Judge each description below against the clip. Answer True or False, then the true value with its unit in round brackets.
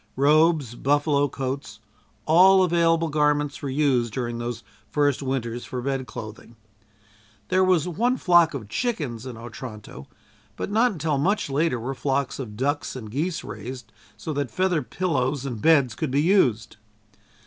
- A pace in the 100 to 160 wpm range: True (150 wpm)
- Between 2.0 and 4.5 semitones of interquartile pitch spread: False (5.0 semitones)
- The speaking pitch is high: False (140 Hz)